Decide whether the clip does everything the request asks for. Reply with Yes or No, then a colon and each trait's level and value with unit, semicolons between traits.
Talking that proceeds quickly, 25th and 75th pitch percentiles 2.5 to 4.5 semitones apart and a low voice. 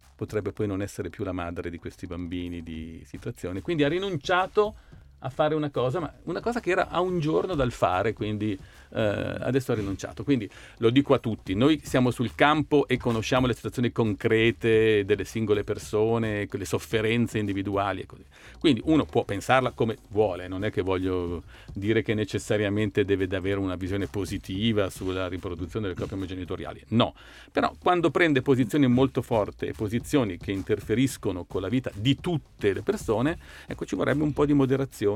No: fast, 175 wpm; wide, 5.4 semitones; low, 110 Hz